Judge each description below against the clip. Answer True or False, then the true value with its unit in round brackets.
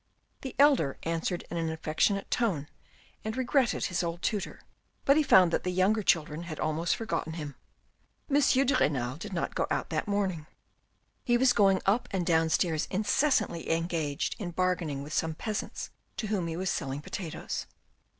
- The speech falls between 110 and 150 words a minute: False (170 wpm)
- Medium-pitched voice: True (175 Hz)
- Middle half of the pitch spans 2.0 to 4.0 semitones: False (4.7 semitones)